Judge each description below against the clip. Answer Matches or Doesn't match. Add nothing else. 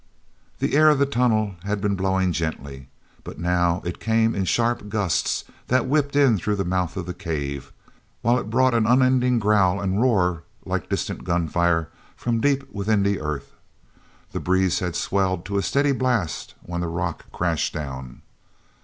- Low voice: Matches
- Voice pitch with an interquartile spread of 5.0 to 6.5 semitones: Matches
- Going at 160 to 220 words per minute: Matches